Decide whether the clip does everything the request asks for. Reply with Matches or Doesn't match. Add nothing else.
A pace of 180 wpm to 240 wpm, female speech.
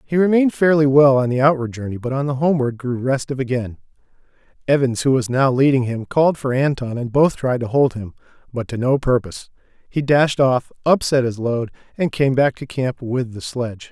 Doesn't match